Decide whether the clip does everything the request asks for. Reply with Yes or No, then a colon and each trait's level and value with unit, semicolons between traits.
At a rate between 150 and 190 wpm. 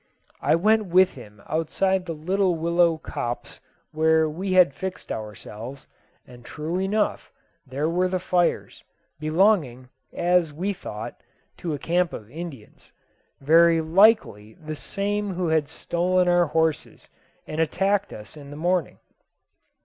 No: slow, 135 wpm